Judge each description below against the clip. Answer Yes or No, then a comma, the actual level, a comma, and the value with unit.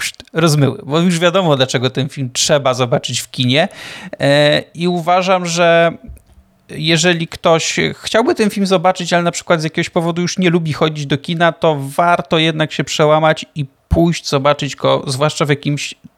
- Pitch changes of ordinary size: Yes, average, 3.4 semitones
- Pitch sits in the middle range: Yes, medium, 160 Hz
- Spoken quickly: Yes, fast, 165 wpm